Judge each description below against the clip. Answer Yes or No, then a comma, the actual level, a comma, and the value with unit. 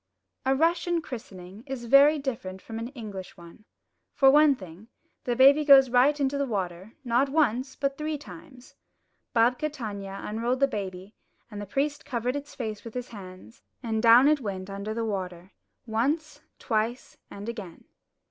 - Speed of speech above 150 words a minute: Yes, average, 165 wpm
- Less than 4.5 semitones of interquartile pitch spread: No, average, 5.2 semitones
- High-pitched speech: Yes, high, 235 Hz